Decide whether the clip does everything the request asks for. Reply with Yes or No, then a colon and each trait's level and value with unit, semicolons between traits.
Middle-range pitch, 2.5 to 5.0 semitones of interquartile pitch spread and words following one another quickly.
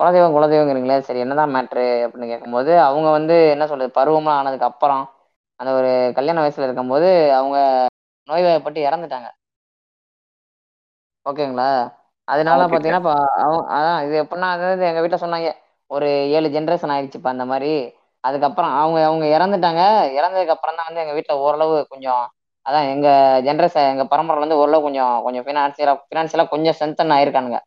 Yes: medium, 150 Hz; average, 3.2 semitones; fast, 140 wpm